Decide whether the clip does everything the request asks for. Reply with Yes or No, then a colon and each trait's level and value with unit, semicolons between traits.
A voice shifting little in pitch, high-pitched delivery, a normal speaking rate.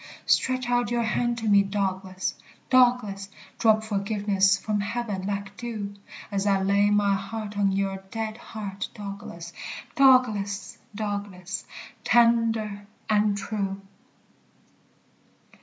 No: narrow, 2.1 semitones; high, 205 Hz; slow, 110 wpm